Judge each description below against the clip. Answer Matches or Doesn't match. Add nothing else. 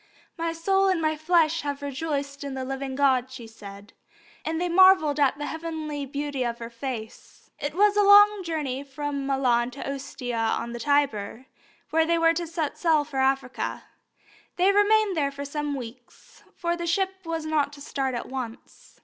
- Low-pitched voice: Doesn't match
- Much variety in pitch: Doesn't match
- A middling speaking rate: Matches